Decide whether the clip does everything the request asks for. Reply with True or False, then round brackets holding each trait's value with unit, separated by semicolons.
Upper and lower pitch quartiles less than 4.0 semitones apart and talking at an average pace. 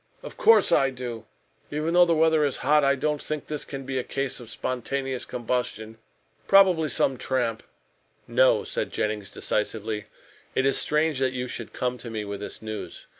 False (4.7 semitones; 180 wpm)